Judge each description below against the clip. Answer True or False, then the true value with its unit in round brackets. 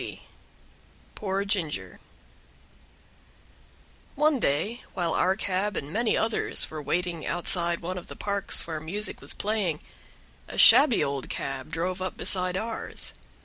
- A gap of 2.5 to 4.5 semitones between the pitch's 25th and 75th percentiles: True (3.8 semitones)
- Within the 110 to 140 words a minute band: True (135 wpm)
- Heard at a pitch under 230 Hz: True (185 Hz)